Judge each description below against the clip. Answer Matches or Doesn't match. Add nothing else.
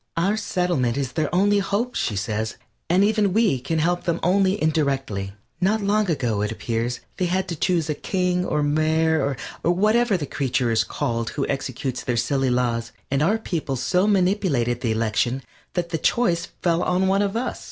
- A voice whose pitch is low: Doesn't match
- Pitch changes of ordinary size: Doesn't match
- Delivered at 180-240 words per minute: Matches